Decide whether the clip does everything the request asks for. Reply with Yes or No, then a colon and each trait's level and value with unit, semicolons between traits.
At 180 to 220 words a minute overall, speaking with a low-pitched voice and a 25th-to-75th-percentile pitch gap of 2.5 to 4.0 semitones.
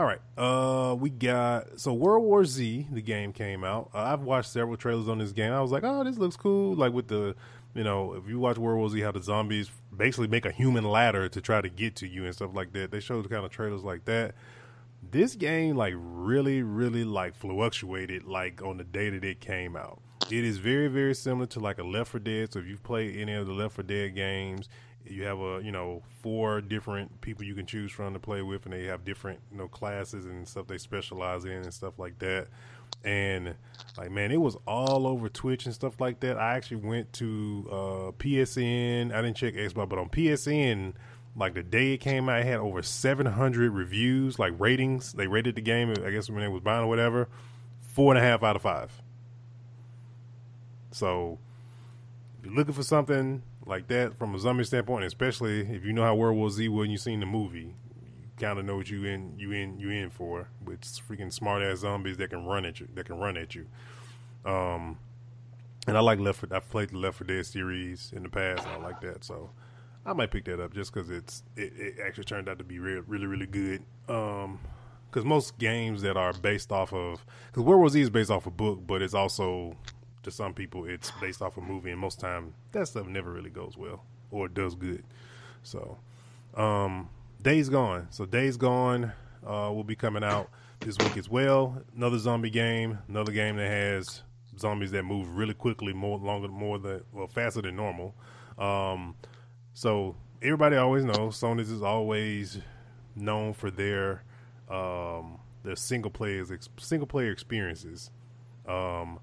Yes: fast, 205 wpm; low, 110 Hz; average, 3.6 semitones